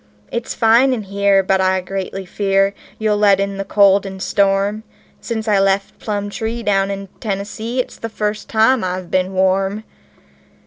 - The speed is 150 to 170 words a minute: Yes, average, 165 wpm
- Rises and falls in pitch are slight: Yes, narrow, 1.9 semitones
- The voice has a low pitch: No, high, 200 Hz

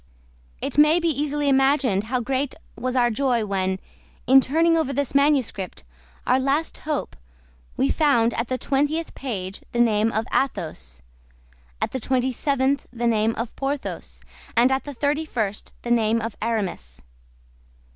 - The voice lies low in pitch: No, very high, 255 Hz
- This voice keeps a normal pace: Yes, average, 155 wpm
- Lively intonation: No, average, 4.0 semitones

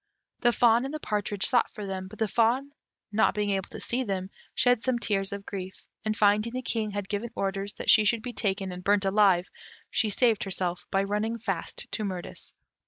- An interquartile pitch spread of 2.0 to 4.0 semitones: Yes, average, 2.9 semitones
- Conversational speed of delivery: No, fast, 210 wpm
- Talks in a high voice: Yes, high, 210 Hz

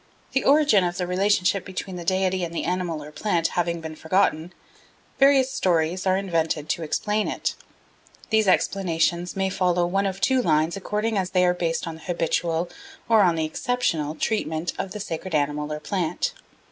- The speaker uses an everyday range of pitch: Yes, average, 3.1 semitones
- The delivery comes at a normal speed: Yes, average, 180 wpm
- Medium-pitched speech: Yes, medium, 180 Hz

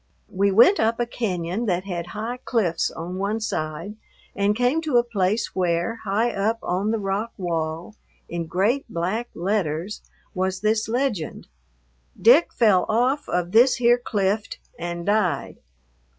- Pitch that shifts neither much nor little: Yes, average, 4.4 semitones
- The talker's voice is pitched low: No, high, 205 Hz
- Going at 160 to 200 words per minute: No, average, 150 wpm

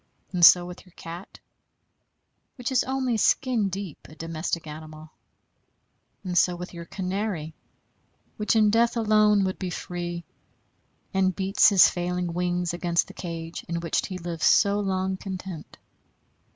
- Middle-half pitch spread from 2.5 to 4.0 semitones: Yes, average, 2.8 semitones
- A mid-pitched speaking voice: Yes, medium, 180 Hz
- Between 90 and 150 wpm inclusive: Yes, average, 145 wpm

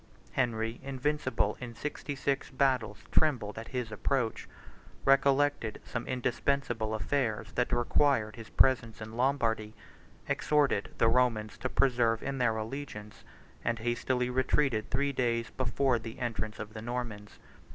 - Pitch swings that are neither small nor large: Yes, average, 3.2 semitones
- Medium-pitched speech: No, low, 120 Hz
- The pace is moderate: No, slow, 130 wpm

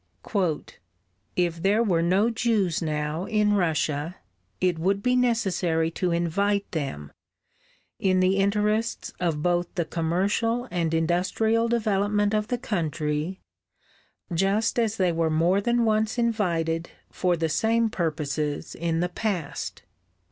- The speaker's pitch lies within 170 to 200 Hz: Yes, medium, 185 Hz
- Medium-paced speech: No, slow, 125 wpm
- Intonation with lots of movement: No, average, 4.5 semitones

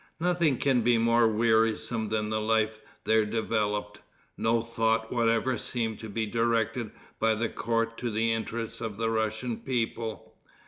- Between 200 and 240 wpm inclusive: No, average, 150 wpm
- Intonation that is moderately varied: No, narrow, 1.0 semitones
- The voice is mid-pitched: No, low, 115 Hz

